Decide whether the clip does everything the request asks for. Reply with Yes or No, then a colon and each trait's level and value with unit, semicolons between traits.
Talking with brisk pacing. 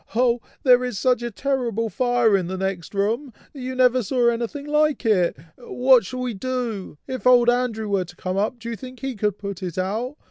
Yes: fast, 210 wpm